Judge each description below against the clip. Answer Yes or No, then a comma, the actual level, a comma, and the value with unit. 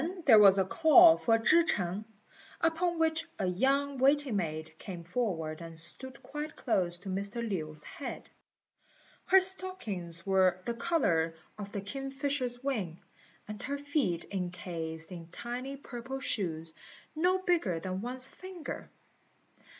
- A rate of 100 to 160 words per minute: Yes, average, 140 wpm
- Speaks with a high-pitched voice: Yes, high, 225 Hz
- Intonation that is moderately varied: No, wide, 8.1 semitones